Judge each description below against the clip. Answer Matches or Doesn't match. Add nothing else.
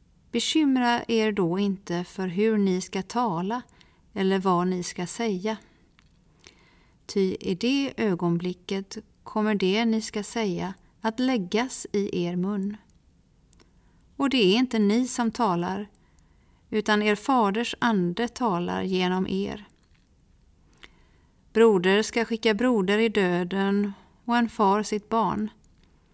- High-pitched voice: Matches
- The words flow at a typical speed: Doesn't match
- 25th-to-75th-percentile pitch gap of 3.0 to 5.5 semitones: Matches